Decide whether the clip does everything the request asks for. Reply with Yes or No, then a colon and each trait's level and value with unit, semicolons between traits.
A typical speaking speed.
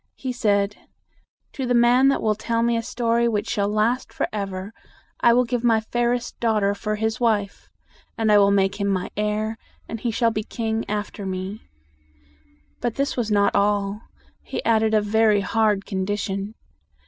Yes: average, 185 wpm